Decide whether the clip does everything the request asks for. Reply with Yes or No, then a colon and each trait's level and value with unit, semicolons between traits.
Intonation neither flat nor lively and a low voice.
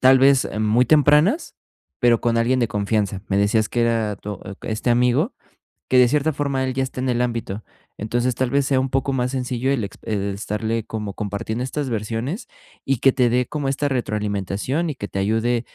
Yes: average, 3.7 semitones; low, 120 Hz